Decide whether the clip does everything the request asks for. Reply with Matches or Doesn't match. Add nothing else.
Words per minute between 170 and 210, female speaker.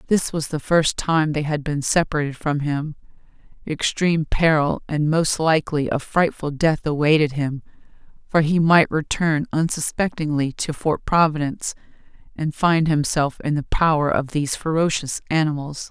Doesn't match